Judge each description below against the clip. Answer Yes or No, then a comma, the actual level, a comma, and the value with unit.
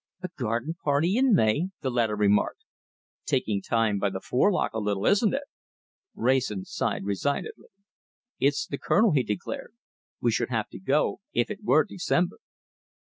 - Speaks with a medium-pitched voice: No, low, 130 Hz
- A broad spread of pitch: Yes, wide, 8.9 semitones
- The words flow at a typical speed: Yes, average, 155 wpm